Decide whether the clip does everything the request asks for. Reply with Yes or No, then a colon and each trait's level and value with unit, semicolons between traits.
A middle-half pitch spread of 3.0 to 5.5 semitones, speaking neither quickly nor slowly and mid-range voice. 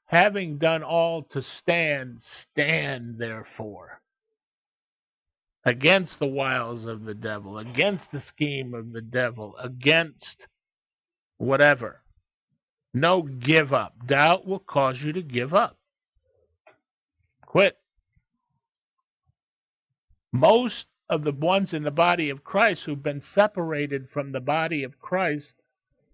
No: average, 4.8 semitones; slow, 115 wpm; medium, 150 Hz